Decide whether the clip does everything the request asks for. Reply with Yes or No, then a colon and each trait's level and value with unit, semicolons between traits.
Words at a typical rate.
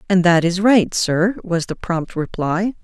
Yes: average, 190 wpm